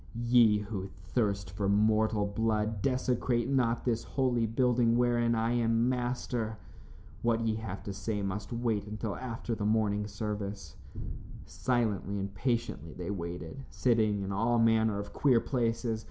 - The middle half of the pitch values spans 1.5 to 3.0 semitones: Yes, narrow, 2.6 semitones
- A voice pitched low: Yes, low, 110 Hz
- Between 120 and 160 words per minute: Yes, average, 145 wpm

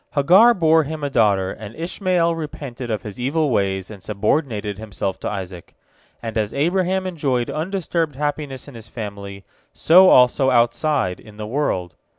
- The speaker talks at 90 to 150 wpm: No, average, 160 wpm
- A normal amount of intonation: No, wide, 7.2 semitones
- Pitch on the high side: No, low, 130 Hz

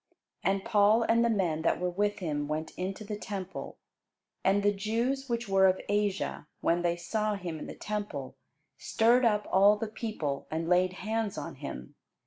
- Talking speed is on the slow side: No, average, 180 wpm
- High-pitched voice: Yes, high, 200 Hz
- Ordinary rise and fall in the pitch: Yes, average, 3.4 semitones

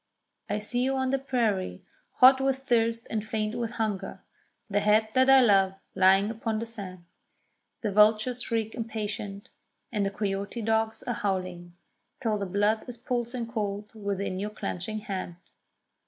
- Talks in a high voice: Yes, high, 215 Hz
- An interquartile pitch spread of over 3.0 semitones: No, average, 2.7 semitones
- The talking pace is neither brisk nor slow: Yes, average, 160 wpm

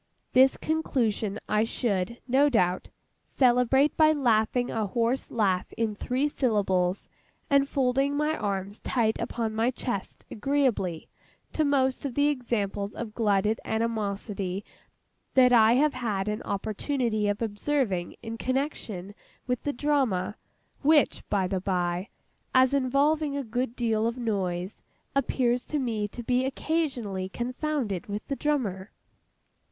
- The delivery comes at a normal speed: No, slow, 130 wpm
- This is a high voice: Yes, high, 235 Hz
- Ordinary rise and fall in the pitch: Yes, average, 4.7 semitones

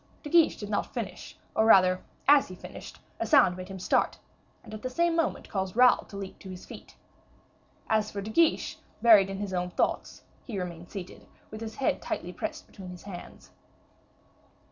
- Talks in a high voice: Yes, high, 200 Hz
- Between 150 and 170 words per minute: No, average, 190 wpm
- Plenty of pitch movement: No, average, 3.7 semitones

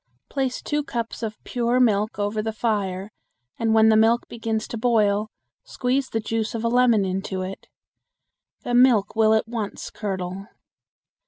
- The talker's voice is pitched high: Yes, high, 220 Hz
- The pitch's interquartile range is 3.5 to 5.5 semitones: No, narrow, 2.4 semitones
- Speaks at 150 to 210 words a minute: Yes, average, 160 wpm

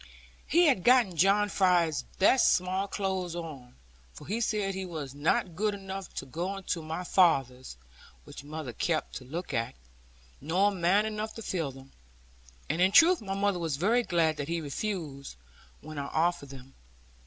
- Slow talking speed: No, average, 170 wpm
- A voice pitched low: No, medium, 175 Hz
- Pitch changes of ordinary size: Yes, average, 4.4 semitones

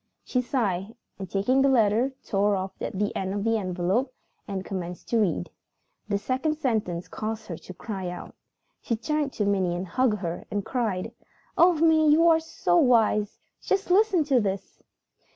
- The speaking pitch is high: Yes, high, 215 Hz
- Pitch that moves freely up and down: Yes, wide, 5.7 semitones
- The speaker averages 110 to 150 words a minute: No, average, 170 wpm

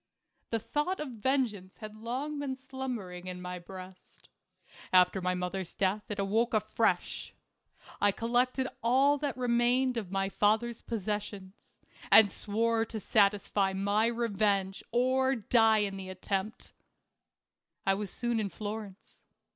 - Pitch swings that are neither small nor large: Yes, average, 3.7 semitones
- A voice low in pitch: No, high, 215 Hz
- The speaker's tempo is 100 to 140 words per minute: Yes, slow, 135 wpm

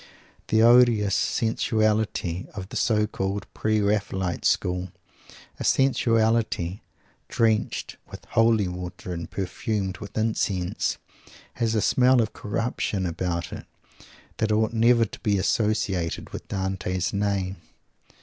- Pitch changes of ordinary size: Yes, average, 3.1 semitones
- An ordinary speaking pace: No, slow, 120 wpm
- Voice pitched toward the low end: Yes, low, 105 Hz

